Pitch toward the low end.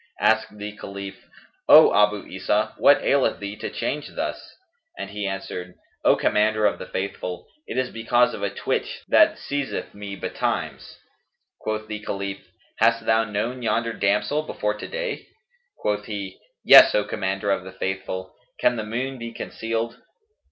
Yes: low, 105 Hz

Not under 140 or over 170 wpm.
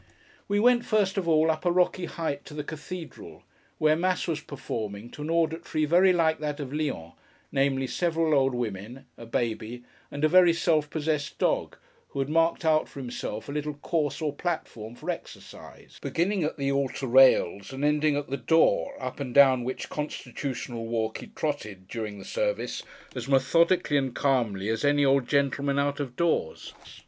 No: average, 180 wpm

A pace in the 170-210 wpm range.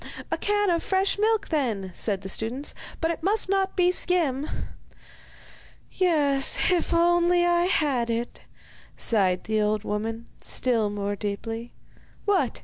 No: average, 140 wpm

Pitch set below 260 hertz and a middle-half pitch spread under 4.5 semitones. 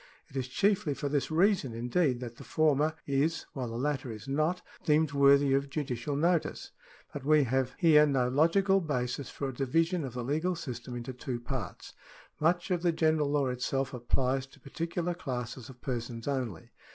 Yes: medium, 140 Hz; average, 4.0 semitones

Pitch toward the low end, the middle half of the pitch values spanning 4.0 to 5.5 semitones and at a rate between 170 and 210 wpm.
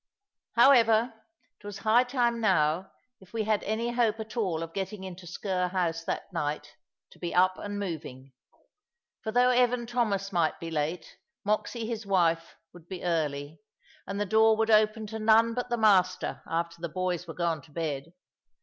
No: high, 195 Hz; average, 4.7 semitones; average, 175 wpm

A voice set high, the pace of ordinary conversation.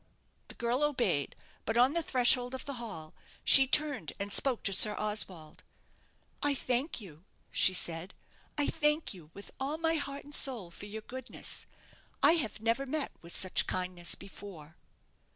Yes: high, 235 Hz; average, 165 wpm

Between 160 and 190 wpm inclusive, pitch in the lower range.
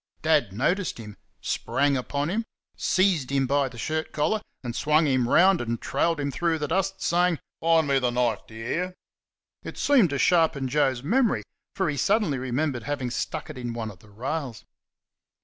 No: average, 185 wpm; medium, 145 Hz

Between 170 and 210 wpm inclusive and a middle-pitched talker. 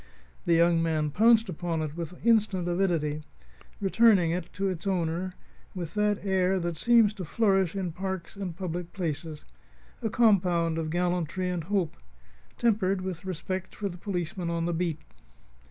No: average, 155 wpm; medium, 180 Hz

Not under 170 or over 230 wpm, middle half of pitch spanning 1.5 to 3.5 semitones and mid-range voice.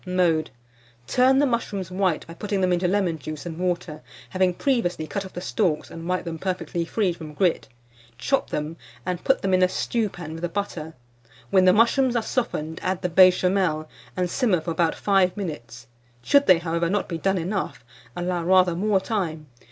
Yes: average, 190 wpm; average, 2.9 semitones; medium, 180 Hz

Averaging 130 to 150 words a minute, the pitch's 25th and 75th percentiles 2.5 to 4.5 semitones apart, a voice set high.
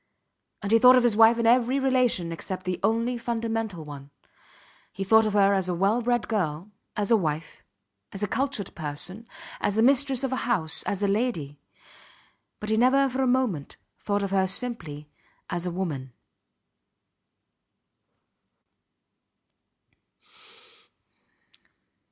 No: average, 140 wpm; average, 5.1 semitones; high, 210 Hz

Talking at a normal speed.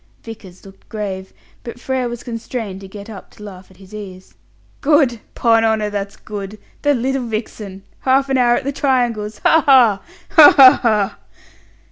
Yes: average, 170 wpm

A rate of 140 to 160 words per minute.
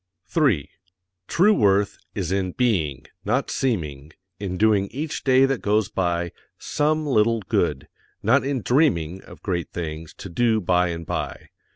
Yes: average, 150 wpm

